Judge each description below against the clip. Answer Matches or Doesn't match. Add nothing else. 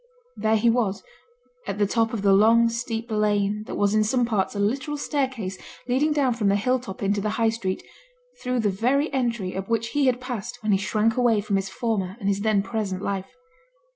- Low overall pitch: Doesn't match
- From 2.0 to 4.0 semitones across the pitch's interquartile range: Matches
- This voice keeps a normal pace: Doesn't match